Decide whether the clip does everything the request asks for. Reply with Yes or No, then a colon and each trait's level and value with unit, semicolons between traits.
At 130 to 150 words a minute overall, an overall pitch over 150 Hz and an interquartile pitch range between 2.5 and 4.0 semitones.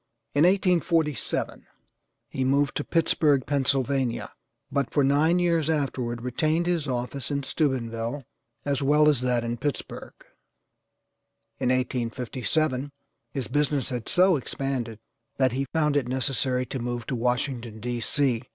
No: slow, 135 wpm; low, 135 Hz; average, 3.2 semitones